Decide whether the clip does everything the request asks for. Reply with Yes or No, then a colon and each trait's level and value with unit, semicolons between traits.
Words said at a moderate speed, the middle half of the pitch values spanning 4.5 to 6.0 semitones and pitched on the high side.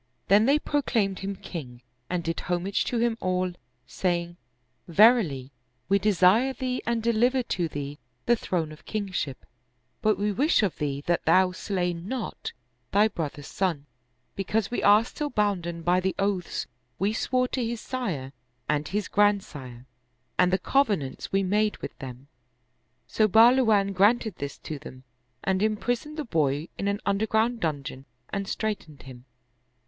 Yes: average, 155 wpm; average, 4.9 semitones; high, 195 Hz